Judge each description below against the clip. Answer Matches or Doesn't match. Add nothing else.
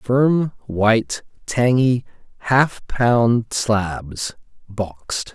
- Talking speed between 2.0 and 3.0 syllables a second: Matches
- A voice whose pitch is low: Matches